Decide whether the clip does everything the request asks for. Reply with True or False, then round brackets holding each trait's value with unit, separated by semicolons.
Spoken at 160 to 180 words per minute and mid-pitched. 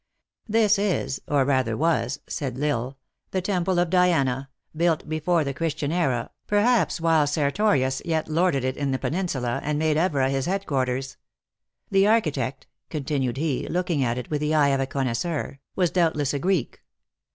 True (175 wpm; 150 Hz)